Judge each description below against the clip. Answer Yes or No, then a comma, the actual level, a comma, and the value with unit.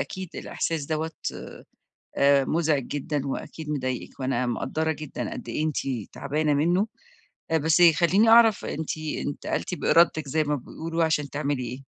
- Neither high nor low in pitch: Yes, medium, 150 Hz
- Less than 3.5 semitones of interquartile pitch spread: Yes, narrow, 2.6 semitones